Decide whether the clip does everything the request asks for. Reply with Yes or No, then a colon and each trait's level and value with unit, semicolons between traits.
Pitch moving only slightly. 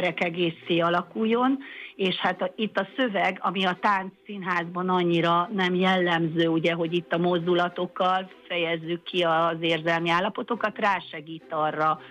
Yes: narrow, 2.2 semitones